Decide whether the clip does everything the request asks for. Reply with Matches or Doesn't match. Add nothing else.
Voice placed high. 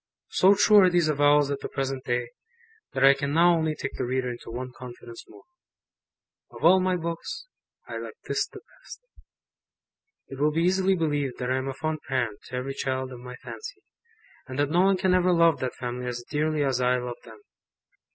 Doesn't match